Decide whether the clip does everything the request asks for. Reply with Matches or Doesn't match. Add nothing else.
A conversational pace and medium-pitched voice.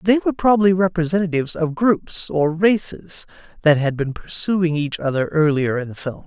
Matches